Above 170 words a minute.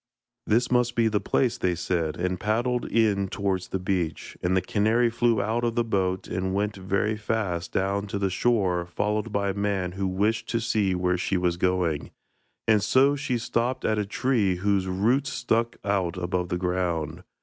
Yes: average, 185 wpm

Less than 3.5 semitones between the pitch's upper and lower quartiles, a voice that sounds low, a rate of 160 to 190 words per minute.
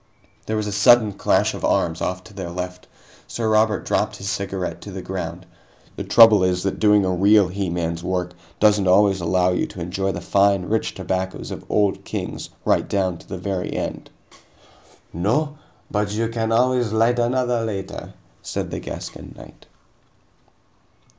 Yes: average, 3.0 semitones; low, 100 Hz; average, 170 wpm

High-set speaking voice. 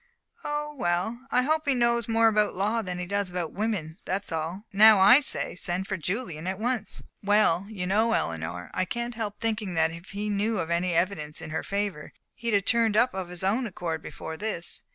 Yes: high, 200 Hz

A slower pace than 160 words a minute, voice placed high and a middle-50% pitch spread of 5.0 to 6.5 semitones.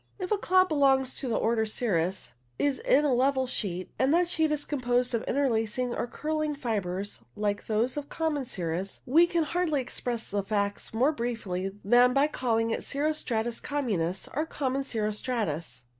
No: average, 175 wpm; high, 245 Hz; average, 5.3 semitones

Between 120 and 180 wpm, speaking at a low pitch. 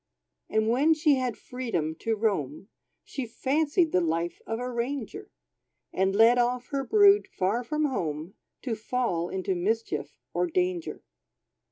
No: average, 145 wpm; high, 240 Hz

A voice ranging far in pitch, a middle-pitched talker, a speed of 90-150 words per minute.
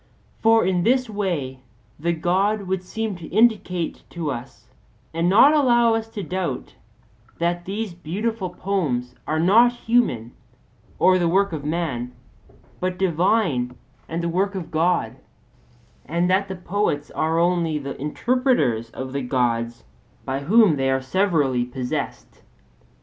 Yes: wide, 6.0 semitones; medium, 175 Hz; average, 140 wpm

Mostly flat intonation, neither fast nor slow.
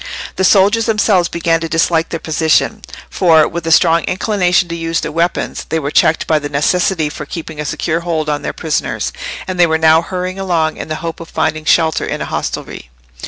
No: narrow, 2.2 semitones; fast, 210 wpm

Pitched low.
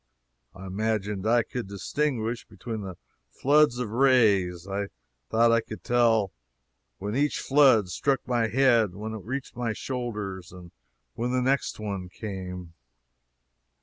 Yes: low, 110 Hz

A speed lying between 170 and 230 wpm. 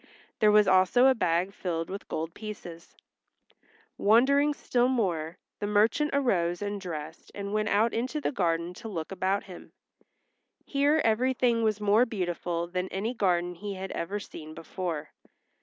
No: average, 155 wpm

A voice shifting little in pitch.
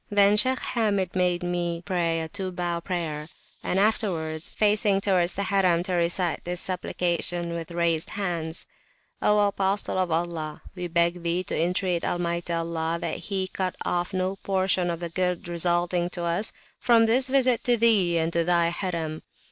Yes: narrow, 2.2 semitones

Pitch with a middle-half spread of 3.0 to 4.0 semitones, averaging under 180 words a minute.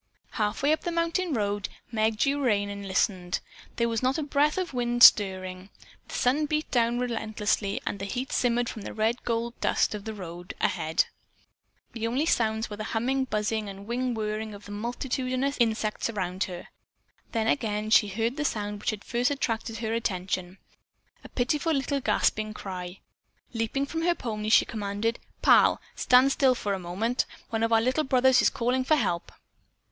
No: average, 3.6 semitones; average, 185 wpm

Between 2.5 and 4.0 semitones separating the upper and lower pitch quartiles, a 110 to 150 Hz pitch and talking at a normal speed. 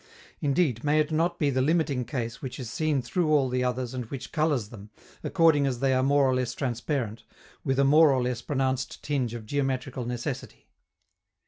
Yes: average, 2.9 semitones; low, 135 Hz; average, 195 wpm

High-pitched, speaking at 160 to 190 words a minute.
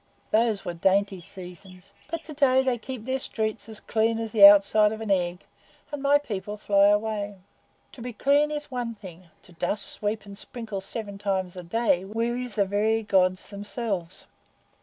Yes: high, 210 Hz; average, 180 wpm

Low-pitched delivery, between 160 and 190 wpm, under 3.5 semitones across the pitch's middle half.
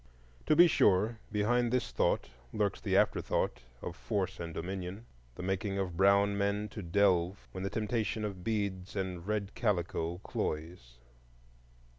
No: very low, 95 Hz; average, 140 wpm; average, 2.9 semitones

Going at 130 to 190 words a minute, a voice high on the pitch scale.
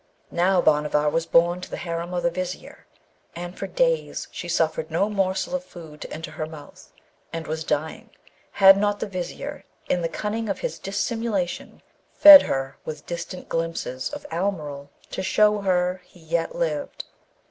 No: average, 170 wpm; medium, 175 Hz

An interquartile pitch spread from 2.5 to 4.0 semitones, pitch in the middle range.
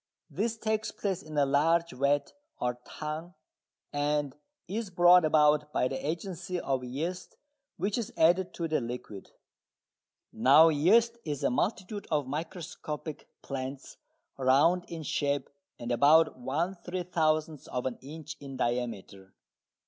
No: average, 4.4 semitones; medium, 155 Hz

